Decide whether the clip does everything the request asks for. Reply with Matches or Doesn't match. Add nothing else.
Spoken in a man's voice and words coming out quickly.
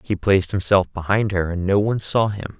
Matches